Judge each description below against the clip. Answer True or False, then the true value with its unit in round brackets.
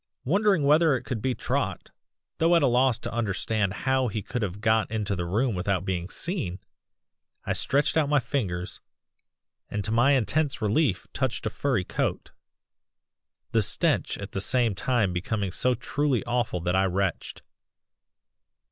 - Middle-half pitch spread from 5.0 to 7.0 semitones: True (5.4 semitones)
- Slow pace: False (160 wpm)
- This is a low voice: True (115 Hz)